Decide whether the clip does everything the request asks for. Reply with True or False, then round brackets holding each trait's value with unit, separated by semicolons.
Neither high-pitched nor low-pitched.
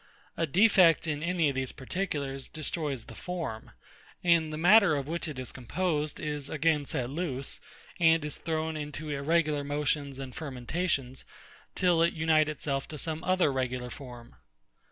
True (150 Hz)